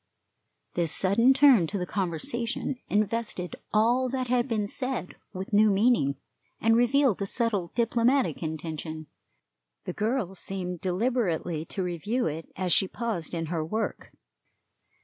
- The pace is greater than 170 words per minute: No, slow, 135 wpm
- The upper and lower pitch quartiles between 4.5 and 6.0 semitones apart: Yes, average, 5.2 semitones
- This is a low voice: No, high, 205 Hz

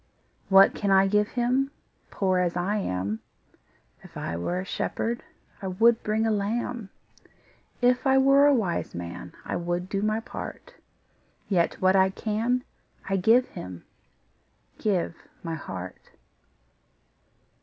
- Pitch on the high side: Yes, high, 195 Hz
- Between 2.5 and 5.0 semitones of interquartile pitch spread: Yes, average, 4.6 semitones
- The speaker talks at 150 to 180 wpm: No, slow, 135 wpm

